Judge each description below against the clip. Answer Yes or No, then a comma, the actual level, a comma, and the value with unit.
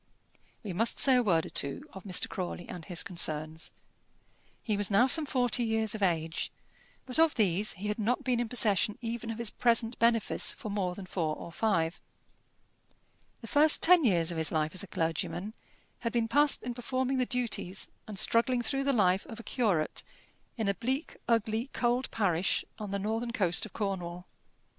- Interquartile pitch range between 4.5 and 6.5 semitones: Yes, average, 4.9 semitones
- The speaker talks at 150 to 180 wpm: No, average, 190 wpm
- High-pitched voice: Yes, high, 215 Hz